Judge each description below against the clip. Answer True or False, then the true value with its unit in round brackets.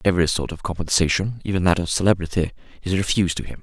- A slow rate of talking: False (200 wpm)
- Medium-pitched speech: False (90 Hz)